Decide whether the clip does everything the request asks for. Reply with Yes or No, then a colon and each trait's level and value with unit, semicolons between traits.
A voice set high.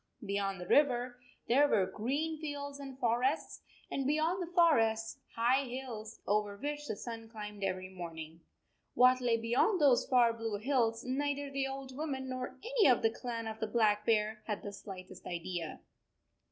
Yes: high, 240 Hz